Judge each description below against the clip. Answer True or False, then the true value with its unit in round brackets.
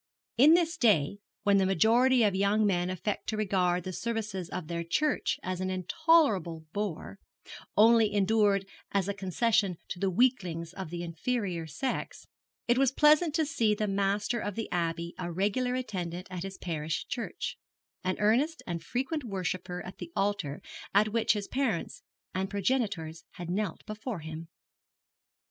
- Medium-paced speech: True (160 wpm)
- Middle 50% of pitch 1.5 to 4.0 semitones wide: False (4.5 semitones)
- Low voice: False (200 Hz)